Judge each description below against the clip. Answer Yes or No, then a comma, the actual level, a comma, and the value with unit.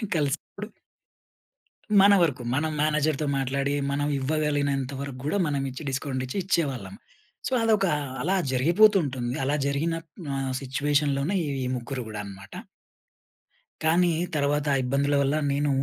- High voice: No, medium, 140 Hz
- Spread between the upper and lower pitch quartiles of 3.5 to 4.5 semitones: No, average, 2.7 semitones